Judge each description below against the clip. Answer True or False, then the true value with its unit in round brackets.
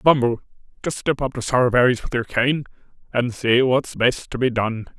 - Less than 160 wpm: False (190 wpm)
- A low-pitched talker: True (125 Hz)